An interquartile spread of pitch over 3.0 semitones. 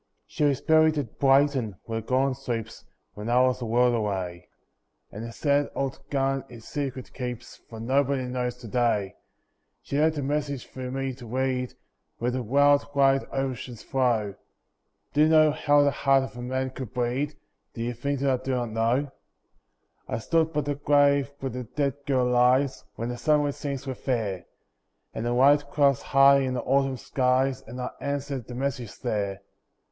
No: narrow, 2.6 semitones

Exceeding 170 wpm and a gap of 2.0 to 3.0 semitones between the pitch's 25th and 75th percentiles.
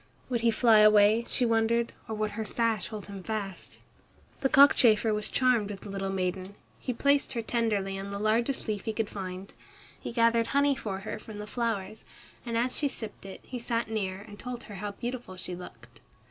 Yes: average, 200 wpm; average, 2.7 semitones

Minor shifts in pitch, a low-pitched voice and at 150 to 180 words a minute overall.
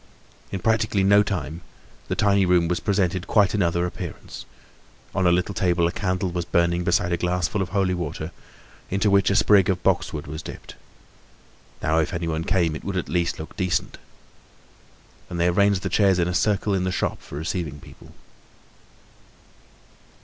Yes: narrow, 2.3 semitones; very low, 90 Hz; average, 170 wpm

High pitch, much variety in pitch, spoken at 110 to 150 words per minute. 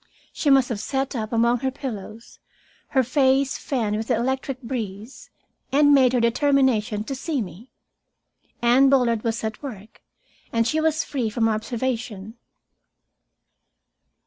No: high, 245 Hz; average, 3.4 semitones; average, 140 wpm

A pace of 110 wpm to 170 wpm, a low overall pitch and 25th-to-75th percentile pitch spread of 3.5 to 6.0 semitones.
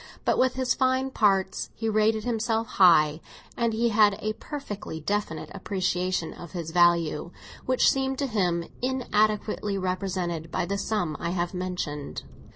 No: average, 150 wpm; high, 200 Hz; average, 4.4 semitones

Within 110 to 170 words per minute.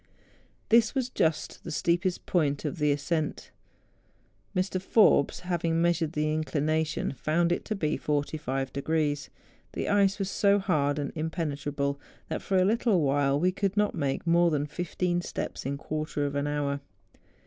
Yes: average, 160 wpm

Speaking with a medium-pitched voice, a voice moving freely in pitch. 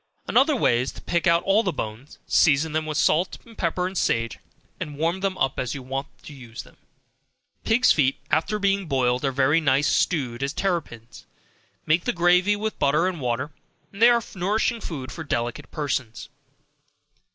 Yes: medium, 155 Hz; wide, 5.8 semitones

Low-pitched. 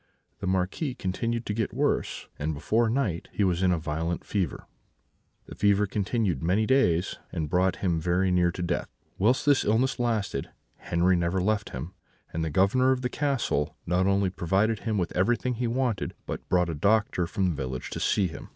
Yes: very low, 95 Hz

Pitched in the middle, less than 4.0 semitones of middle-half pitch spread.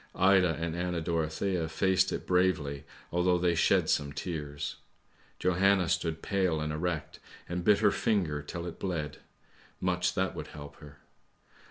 No: very low, 85 Hz; average, 2.9 semitones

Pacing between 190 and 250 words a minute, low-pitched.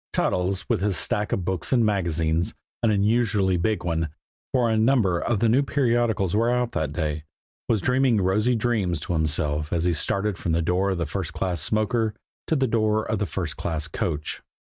Yes: average, 195 wpm; low, 100 Hz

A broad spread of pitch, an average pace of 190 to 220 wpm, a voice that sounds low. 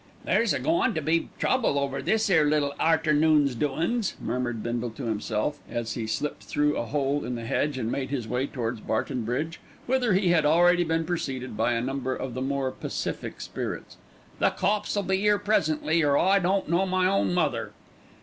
No: wide, 5.7 semitones; average, 195 wpm; medium, 150 Hz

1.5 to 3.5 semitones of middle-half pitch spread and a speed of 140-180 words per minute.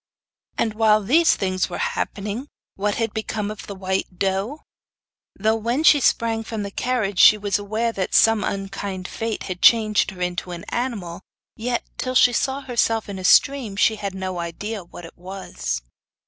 Yes: average, 3.1 semitones; average, 175 wpm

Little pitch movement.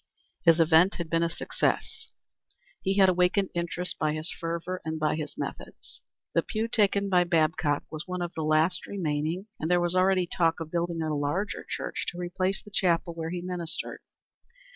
Yes: narrow, 2.3 semitones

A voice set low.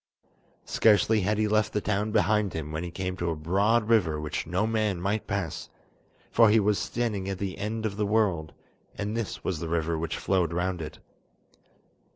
Yes: low, 100 Hz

